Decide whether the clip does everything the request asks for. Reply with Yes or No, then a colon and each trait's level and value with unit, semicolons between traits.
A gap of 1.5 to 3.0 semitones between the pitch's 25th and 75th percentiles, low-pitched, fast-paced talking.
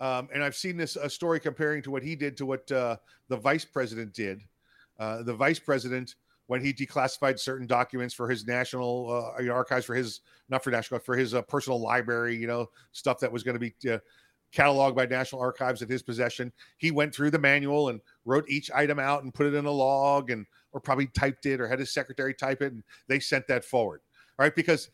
Yes: narrow, 2.4 semitones; low, 130 Hz; fast, 230 wpm